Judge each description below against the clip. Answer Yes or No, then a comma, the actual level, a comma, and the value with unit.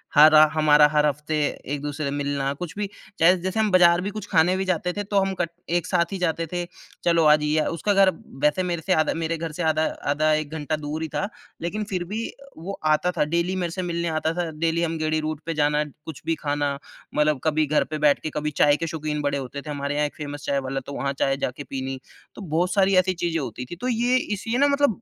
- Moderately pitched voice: Yes, medium, 160 Hz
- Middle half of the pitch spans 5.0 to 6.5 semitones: No, average, 3.3 semitones